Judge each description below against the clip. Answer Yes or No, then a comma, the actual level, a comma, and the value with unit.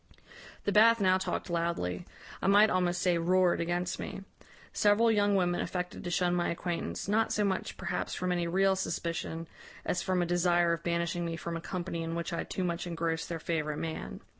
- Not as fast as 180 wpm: No, average, 195 wpm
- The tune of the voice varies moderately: No, narrow, 1.8 semitones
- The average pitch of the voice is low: No, medium, 175 Hz